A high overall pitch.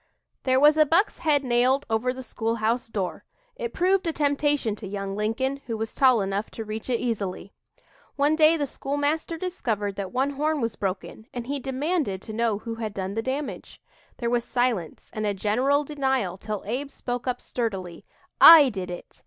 Yes: high, 245 Hz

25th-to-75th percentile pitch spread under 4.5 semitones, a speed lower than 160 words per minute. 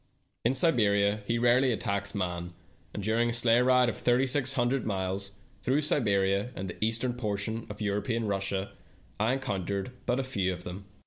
No: average, 3.8 semitones; average, 170 wpm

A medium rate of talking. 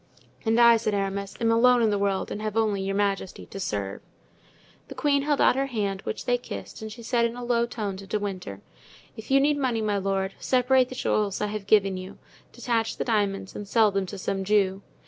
No: fast, 230 wpm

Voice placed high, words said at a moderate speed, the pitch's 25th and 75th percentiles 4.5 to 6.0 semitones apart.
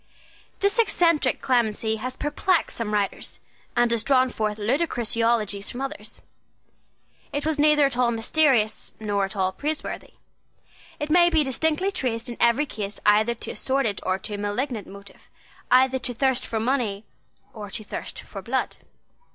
Yes: high, 240 Hz; average, 160 wpm; average, 5.2 semitones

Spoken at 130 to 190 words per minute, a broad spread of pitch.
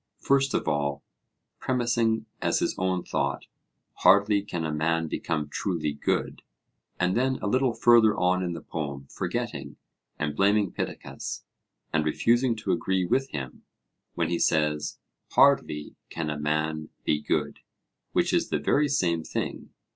Yes: average, 145 wpm; wide, 6.4 semitones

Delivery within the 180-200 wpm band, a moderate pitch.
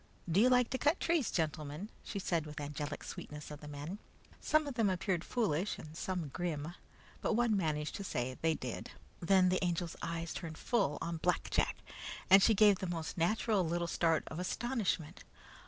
Yes: average, 190 wpm; medium, 175 Hz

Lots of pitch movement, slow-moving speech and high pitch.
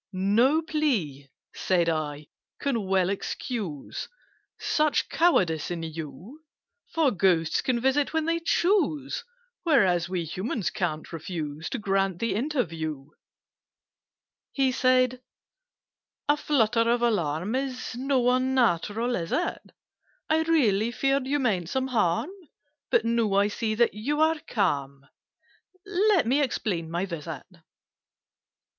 Yes: wide, 7.8 semitones; slow, 120 wpm; high, 225 Hz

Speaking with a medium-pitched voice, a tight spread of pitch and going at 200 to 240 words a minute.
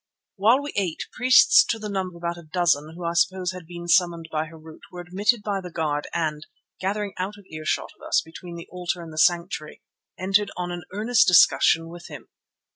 No: medium, 175 Hz; average, 3.0 semitones; fast, 205 wpm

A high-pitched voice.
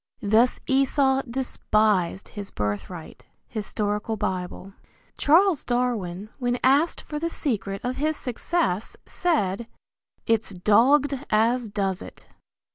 Yes: high, 230 Hz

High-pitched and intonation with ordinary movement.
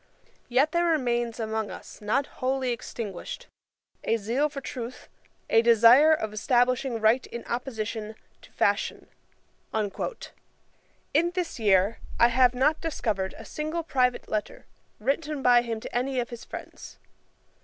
Yes: high, 245 Hz; average, 3.5 semitones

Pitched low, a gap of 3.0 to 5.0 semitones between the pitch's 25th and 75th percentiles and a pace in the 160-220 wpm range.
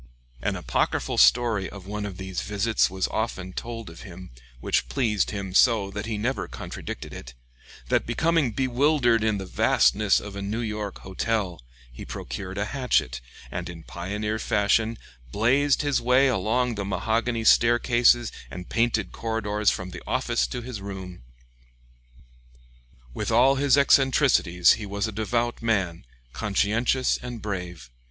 No: low, 110 Hz; average, 3.7 semitones; average, 145 wpm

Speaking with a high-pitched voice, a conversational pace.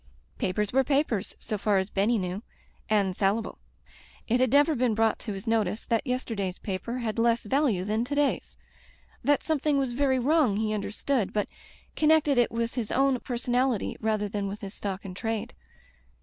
Yes: high, 225 Hz; average, 175 wpm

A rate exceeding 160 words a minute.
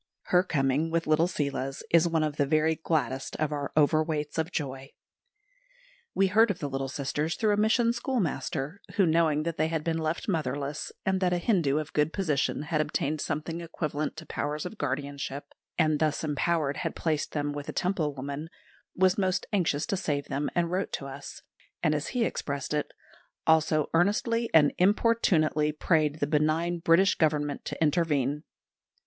Yes: average, 175 wpm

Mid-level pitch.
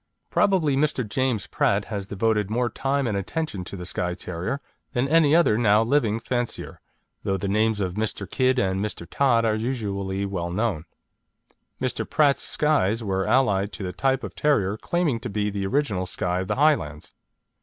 No: low, 110 Hz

